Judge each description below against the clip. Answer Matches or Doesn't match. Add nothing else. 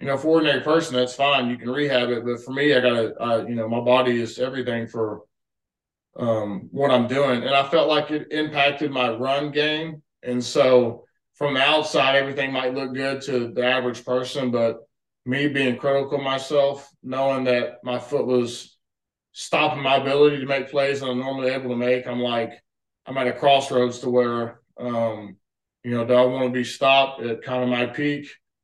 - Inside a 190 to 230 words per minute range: Matches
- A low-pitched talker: Matches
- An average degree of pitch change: Doesn't match